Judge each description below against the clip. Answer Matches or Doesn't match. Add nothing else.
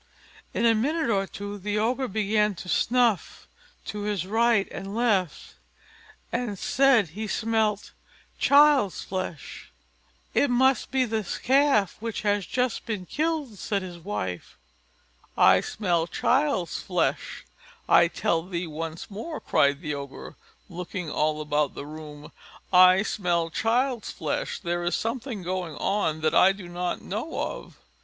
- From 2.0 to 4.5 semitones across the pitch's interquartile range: Doesn't match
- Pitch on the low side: Doesn't match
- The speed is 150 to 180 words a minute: Doesn't match